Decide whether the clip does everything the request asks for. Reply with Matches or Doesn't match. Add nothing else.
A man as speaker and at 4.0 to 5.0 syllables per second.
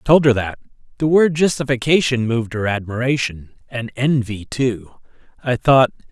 Matches